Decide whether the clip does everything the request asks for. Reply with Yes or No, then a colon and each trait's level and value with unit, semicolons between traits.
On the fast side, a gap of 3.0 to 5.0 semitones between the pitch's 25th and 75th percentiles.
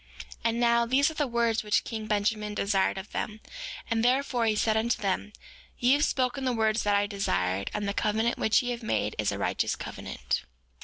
No: fast, 210 wpm; narrow, 2.6 semitones